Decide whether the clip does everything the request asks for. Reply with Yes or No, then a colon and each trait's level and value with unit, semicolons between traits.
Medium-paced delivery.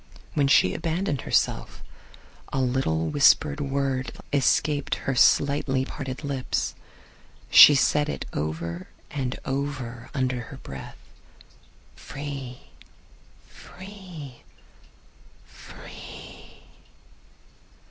No: slow, 85 wpm